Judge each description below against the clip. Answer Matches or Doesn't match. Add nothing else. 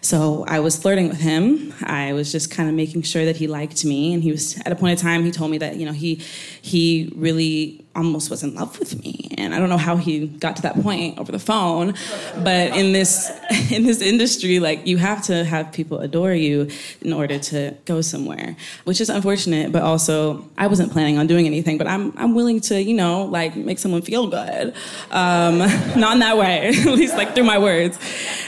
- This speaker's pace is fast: Matches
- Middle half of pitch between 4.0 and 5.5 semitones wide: Doesn't match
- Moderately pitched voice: Matches